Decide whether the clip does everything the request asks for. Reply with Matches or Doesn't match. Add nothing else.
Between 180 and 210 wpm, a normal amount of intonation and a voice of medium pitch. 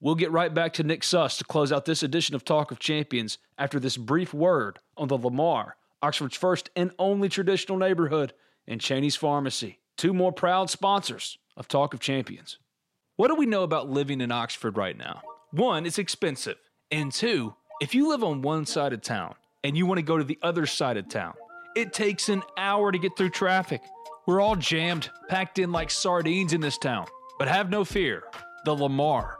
Matches